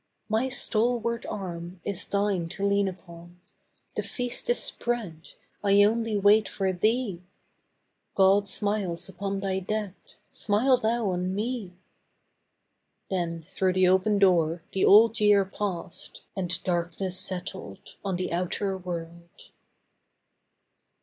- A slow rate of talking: Yes, slow, 120 wpm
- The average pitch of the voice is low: No, high, 195 Hz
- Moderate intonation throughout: Yes, average, 3.0 semitones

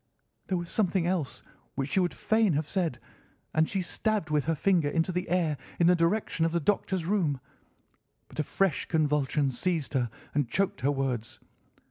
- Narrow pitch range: No, average, 4.2 semitones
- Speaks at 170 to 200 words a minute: Yes, average, 180 wpm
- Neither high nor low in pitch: Yes, medium, 165 Hz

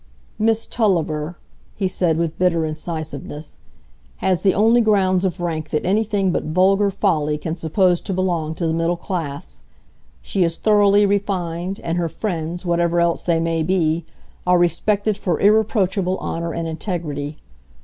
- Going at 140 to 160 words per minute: Yes, average, 150 wpm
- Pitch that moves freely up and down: No, average, 3.2 semitones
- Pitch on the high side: No, medium, 175 Hz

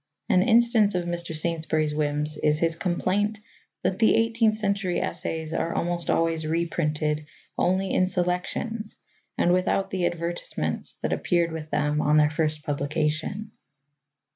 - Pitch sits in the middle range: Yes, medium, 170 Hz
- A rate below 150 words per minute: Yes, average, 140 wpm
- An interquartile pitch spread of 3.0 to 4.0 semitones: Yes, average, 3.6 semitones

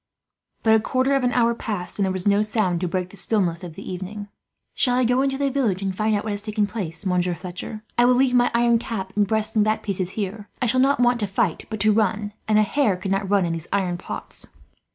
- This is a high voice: Yes, high, 210 Hz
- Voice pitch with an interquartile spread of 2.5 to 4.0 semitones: Yes, average, 3.7 semitones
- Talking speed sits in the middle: No, fast, 260 wpm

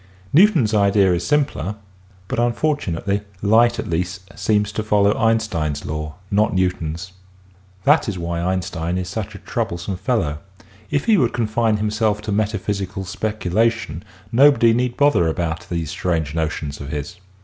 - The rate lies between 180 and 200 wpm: No, average, 145 wpm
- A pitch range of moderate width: Yes, average, 4.7 semitones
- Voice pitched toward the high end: No, low, 100 Hz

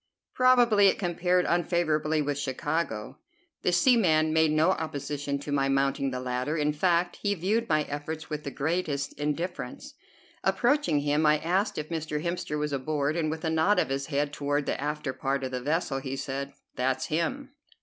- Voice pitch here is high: No, medium, 150 Hz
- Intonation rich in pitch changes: No, average, 3.4 semitones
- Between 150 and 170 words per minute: No, average, 180 wpm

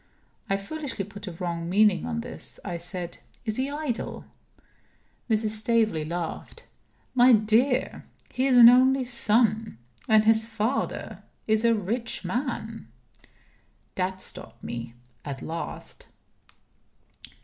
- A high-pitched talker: Yes, high, 220 Hz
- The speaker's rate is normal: No, slow, 120 wpm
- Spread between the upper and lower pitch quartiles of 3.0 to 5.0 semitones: Yes, average, 4.4 semitones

